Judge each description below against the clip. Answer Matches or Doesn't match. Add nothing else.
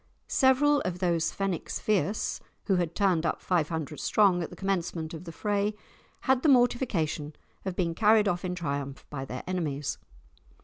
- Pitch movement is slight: Doesn't match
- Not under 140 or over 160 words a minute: Doesn't match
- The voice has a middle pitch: Matches